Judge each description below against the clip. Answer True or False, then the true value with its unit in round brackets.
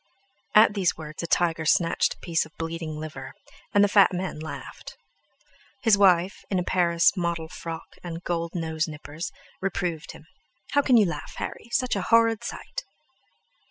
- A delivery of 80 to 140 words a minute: False (165 wpm)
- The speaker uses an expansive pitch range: False (3.4 semitones)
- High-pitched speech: False (170 Hz)